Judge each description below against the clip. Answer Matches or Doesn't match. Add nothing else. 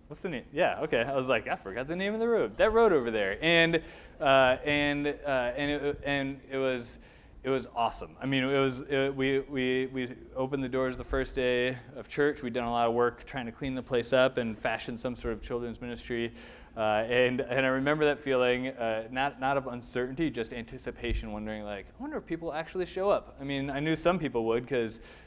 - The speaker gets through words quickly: Matches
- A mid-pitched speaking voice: Doesn't match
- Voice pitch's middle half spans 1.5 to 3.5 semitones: Matches